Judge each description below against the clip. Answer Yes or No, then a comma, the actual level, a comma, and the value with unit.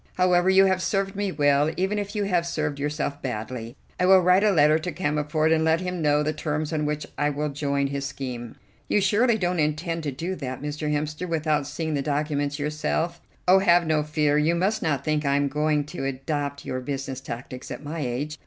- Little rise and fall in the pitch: No, average, 3.2 semitones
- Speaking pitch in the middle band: Yes, medium, 150 Hz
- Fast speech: Yes, fast, 215 wpm